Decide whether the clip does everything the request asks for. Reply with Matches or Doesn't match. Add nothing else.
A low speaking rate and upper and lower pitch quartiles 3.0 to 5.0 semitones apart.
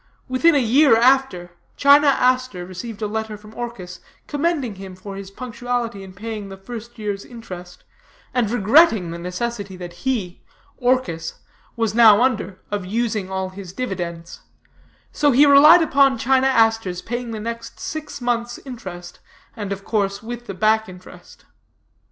Doesn't match